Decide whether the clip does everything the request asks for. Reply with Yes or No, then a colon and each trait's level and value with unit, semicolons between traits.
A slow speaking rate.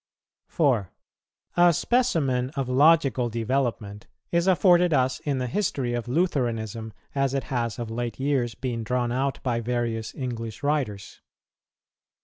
Yes: slow, 130 wpm